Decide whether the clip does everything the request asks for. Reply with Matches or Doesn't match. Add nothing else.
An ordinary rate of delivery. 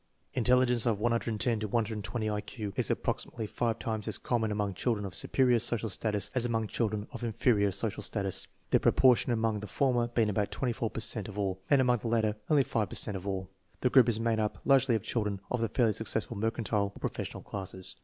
Doesn't match